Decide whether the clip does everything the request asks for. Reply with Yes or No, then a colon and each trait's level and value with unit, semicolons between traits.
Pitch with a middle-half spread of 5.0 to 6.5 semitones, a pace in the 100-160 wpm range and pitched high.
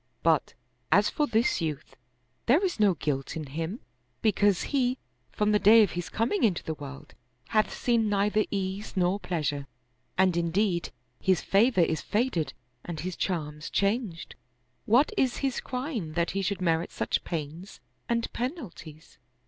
Yes: wide, 5.5 semitones; average, 155 wpm; high, 195 Hz